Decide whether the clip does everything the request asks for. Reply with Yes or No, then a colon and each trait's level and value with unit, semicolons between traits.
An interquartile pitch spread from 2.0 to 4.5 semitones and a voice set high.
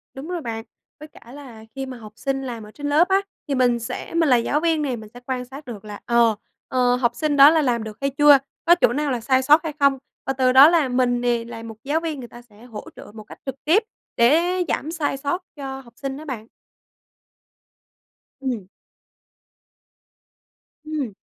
Yes: average, 3.7 semitones; very high, 265 Hz